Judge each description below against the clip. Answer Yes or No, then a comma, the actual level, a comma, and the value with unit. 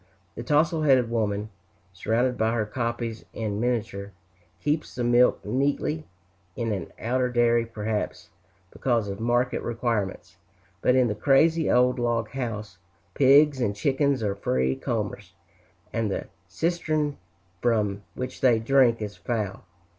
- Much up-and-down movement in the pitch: No, average, 3.5 semitones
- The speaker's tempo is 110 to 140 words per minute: Yes, slow, 135 wpm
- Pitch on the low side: Yes, low, 120 Hz